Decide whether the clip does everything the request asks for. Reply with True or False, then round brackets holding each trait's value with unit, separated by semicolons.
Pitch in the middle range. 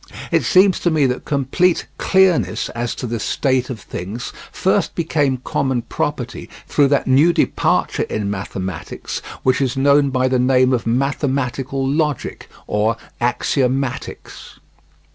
False (130 Hz)